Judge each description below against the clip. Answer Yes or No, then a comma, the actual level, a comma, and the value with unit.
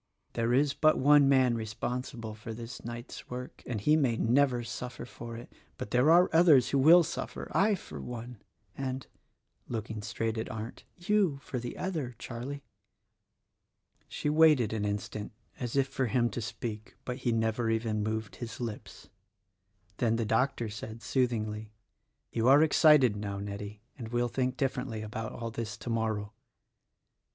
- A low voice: Yes, low, 120 Hz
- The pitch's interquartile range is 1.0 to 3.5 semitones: Yes, average, 3.2 semitones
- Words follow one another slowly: No, average, 165 wpm